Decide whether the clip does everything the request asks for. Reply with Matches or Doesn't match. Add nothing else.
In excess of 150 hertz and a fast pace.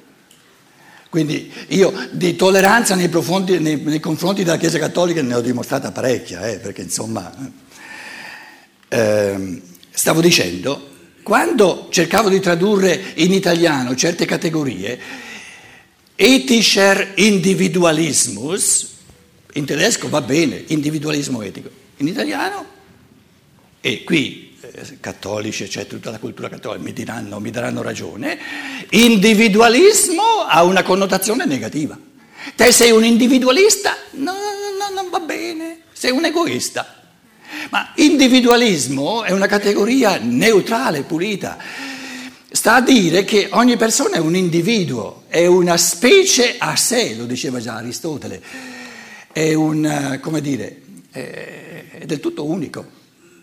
Doesn't match